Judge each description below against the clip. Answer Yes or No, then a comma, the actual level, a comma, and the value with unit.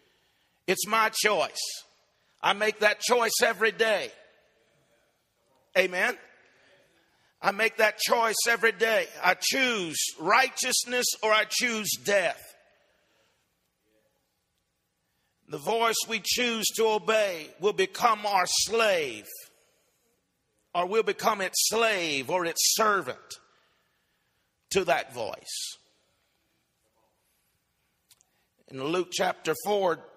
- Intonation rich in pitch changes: No, average, 4.0 semitones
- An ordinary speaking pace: No, slow, 95 wpm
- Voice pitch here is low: No, high, 225 Hz